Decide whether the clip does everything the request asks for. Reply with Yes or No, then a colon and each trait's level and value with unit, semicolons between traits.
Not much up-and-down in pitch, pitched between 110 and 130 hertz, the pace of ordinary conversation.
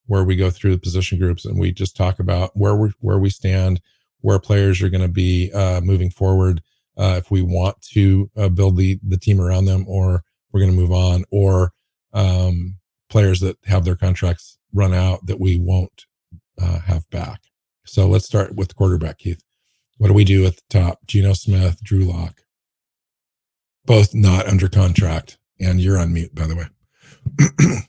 No: narrow, 1.7 semitones; very low, 95 Hz; average, 190 wpm